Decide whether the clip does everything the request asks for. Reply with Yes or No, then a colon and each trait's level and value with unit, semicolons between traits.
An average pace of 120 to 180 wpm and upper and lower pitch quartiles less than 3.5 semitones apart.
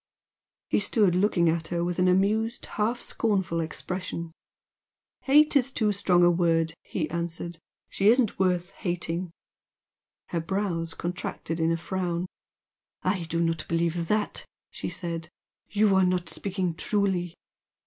Yes: average, 140 wpm; average, 3.0 semitones